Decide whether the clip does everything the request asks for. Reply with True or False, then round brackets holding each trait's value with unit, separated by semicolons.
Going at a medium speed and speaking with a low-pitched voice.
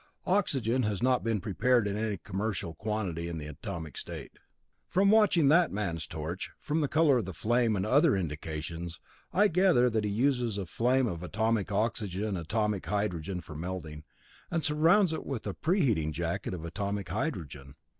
True (170 wpm; 105 Hz)